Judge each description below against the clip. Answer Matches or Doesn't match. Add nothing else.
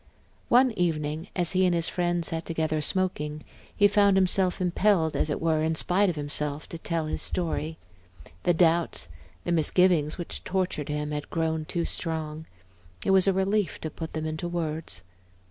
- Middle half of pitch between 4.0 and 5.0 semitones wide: Doesn't match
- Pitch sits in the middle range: Matches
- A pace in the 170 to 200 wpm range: Matches